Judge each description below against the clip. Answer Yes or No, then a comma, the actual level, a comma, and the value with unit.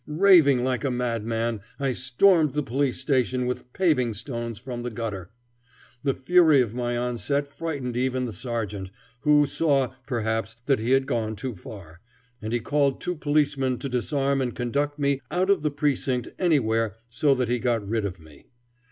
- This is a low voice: Yes, low, 125 Hz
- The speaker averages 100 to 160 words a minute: No, average, 175 wpm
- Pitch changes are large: No, average, 3.5 semitones